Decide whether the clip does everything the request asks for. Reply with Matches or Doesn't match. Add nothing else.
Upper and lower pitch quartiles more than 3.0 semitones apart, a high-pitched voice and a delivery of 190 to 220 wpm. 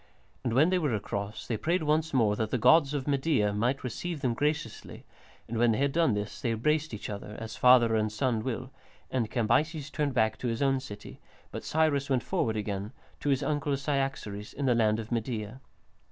Doesn't match